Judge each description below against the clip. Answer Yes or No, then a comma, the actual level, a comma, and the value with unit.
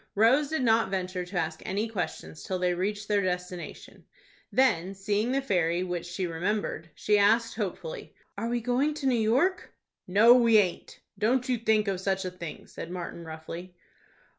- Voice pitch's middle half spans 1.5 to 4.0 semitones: No, average, 4.4 semitones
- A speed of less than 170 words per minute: No, average, 175 wpm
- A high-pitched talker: Yes, high, 200 Hz